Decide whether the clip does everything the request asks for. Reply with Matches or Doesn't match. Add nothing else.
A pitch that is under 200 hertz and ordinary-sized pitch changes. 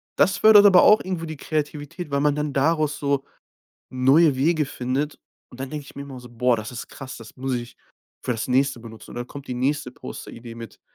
Matches